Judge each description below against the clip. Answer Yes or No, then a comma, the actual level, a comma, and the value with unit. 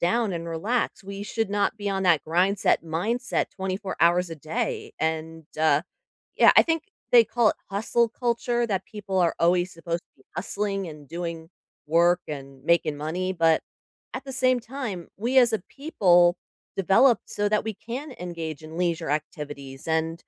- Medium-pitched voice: Yes, medium, 180 Hz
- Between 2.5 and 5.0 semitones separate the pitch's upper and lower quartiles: No, wide, 5.4 semitones